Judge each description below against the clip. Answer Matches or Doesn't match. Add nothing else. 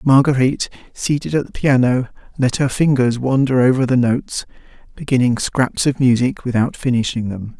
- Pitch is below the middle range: Matches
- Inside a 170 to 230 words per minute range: Doesn't match